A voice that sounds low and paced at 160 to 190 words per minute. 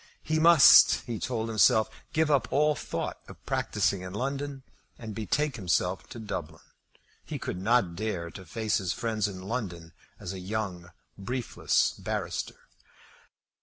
No: low, 110 Hz; average, 145 wpm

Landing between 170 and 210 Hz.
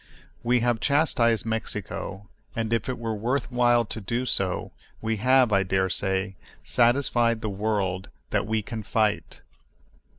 No: low, 110 Hz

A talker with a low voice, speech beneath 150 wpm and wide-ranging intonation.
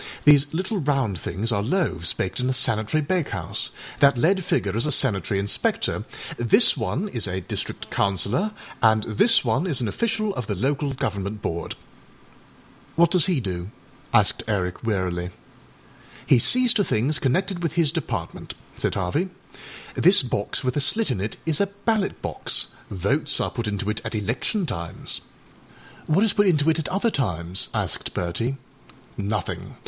No: low, 130 Hz; average, 165 wpm; wide, 8.8 semitones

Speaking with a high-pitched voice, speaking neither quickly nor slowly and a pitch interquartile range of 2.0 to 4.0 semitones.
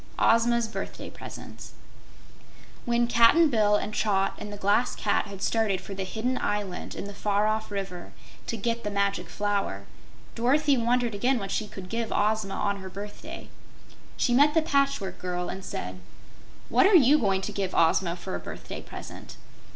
Yes: high, 210 Hz; average, 175 wpm; average, 3.3 semitones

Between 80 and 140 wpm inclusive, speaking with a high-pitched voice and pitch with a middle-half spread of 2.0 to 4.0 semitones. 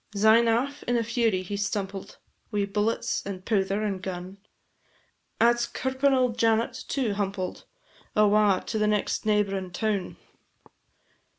Yes: slow, 135 wpm; high, 210 Hz; average, 2.8 semitones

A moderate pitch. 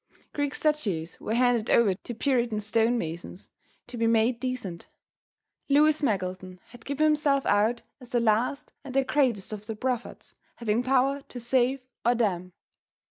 No: high, 240 Hz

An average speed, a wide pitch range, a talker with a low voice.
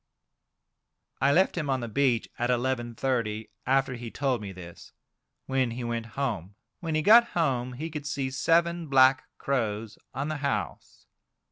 No: average, 155 wpm; average, 3.3 semitones; low, 130 Hz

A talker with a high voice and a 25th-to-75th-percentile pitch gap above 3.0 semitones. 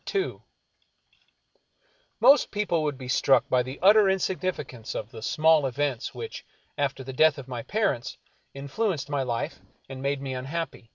No: medium, 140 Hz; average, 4.8 semitones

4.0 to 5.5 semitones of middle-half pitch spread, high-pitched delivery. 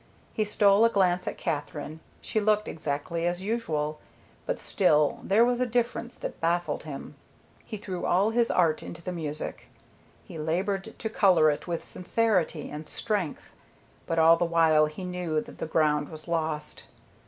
No: average, 4.8 semitones; medium, 175 Hz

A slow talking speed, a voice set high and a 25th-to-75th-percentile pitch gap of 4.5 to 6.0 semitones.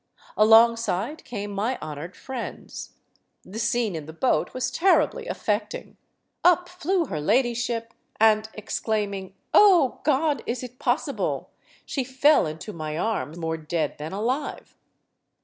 Yes: slow, 130 wpm; high, 225 Hz; wide, 5.5 semitones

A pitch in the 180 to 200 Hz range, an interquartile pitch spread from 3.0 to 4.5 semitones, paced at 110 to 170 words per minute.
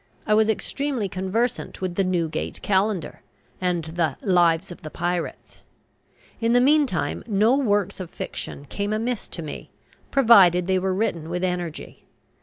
Yes: high, 190 Hz; average, 3.9 semitones; average, 150 wpm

